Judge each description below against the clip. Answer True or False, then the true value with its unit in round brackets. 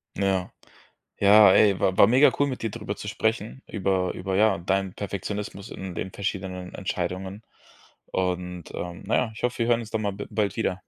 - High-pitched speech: False (100 Hz)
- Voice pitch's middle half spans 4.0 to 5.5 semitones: False (2.6 semitones)